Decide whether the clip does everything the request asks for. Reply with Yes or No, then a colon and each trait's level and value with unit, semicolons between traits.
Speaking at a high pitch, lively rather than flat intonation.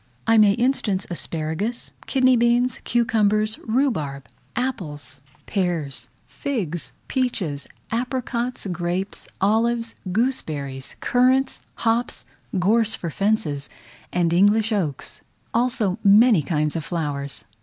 Yes: high, 205 Hz; wide, 6.5 semitones